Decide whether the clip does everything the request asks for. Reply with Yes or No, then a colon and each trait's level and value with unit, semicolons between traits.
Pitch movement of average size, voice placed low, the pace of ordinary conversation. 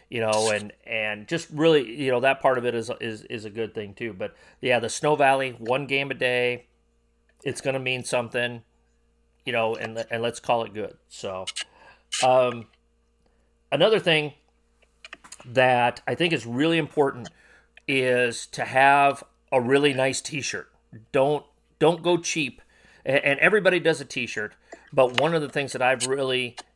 Yes: average, 3.6 semitones; low, 125 Hz; average, 170 wpm